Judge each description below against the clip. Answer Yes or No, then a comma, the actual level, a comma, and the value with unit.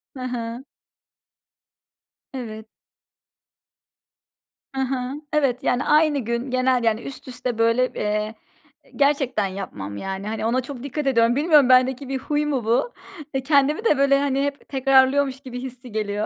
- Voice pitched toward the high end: Yes, very high, 255 Hz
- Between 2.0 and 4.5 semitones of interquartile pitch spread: Yes, average, 3.1 semitones